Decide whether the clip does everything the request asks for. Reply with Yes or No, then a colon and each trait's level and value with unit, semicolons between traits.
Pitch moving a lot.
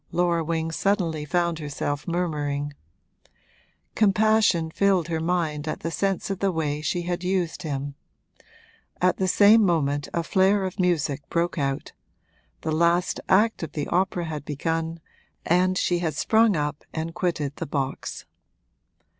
No: average, 3.3 semitones